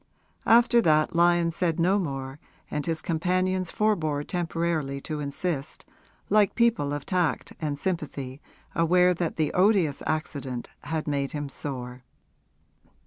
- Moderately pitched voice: Yes, medium, 160 Hz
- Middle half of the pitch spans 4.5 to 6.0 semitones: No, average, 3.9 semitones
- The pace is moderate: No, slow, 130 wpm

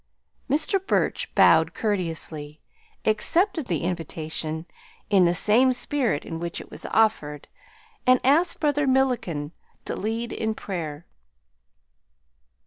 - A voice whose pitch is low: No, high, 210 Hz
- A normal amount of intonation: No, wide, 8.1 semitones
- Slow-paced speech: Yes, slow, 115 wpm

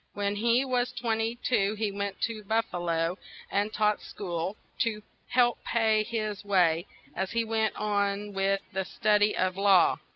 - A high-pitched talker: Yes, high, 210 Hz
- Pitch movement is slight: Yes, narrow, 2.3 semitones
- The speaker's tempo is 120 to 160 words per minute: No, average, 175 wpm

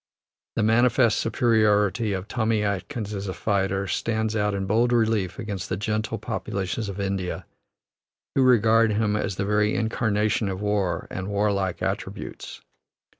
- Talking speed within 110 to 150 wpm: Yes, average, 145 wpm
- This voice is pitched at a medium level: No, low, 105 Hz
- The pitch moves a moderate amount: No, narrow, 2.2 semitones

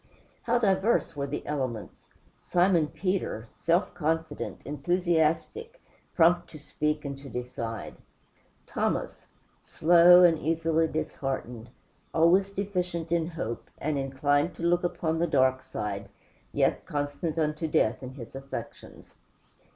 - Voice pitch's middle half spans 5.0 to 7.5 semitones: No, average, 3.9 semitones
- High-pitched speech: No, medium, 160 Hz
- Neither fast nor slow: No, slow, 120 wpm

